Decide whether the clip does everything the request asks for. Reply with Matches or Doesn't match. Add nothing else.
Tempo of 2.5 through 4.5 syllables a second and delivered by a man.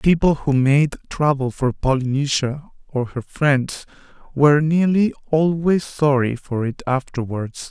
Matches